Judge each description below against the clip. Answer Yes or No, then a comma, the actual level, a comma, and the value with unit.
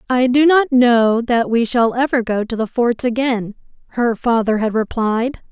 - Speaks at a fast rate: No, average, 185 wpm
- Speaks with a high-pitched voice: Yes, high, 240 Hz